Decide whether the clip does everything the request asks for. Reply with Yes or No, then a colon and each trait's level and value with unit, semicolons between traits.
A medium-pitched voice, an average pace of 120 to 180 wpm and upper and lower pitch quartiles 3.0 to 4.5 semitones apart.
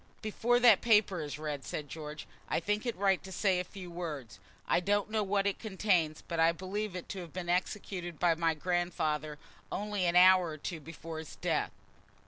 No: medium, 180 Hz; average, 200 wpm; average, 3.7 semitones